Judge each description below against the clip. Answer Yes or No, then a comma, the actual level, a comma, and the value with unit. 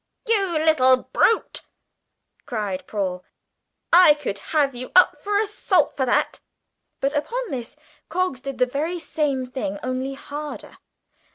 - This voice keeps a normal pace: No, slow, 130 wpm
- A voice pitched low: No, very high, 280 Hz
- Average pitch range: Yes, average, 5.0 semitones